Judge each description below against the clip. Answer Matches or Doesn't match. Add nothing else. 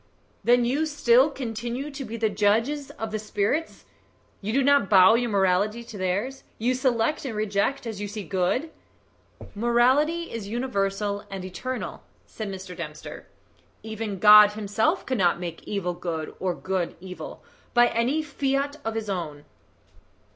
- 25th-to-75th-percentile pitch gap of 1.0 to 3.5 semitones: Doesn't match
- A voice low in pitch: Doesn't match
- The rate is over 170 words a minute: Doesn't match